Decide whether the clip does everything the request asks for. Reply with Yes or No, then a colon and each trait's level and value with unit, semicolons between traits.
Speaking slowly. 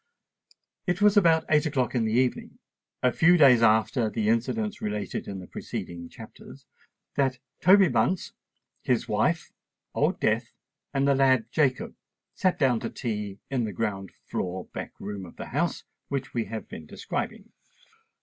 No: average, 160 wpm